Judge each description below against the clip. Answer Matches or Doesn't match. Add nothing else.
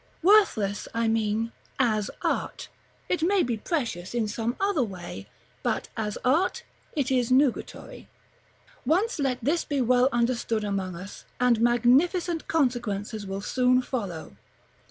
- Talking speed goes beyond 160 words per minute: Doesn't match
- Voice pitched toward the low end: Doesn't match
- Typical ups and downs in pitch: Matches